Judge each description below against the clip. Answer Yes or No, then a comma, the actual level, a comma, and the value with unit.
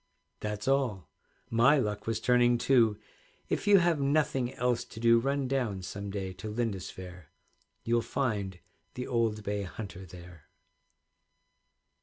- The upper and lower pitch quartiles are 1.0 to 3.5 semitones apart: No, average, 4.2 semitones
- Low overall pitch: Yes, low, 115 Hz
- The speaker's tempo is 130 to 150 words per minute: Yes, slow, 135 wpm